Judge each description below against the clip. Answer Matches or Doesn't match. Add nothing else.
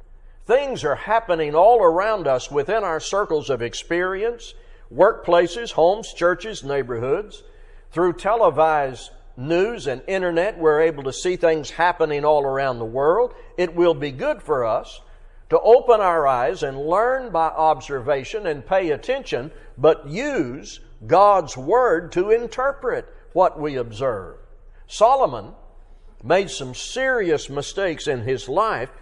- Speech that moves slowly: Matches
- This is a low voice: Doesn't match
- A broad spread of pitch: Matches